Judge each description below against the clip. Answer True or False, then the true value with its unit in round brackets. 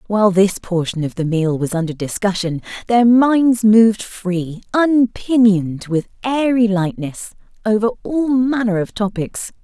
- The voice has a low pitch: False (210 Hz)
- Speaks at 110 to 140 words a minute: True (135 wpm)